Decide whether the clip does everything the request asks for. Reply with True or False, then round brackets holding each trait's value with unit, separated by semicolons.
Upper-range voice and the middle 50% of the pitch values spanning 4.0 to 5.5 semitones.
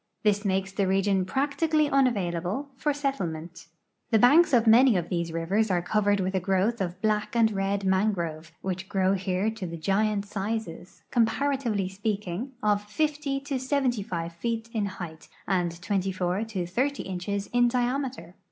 True (205 Hz; 4.5 semitones)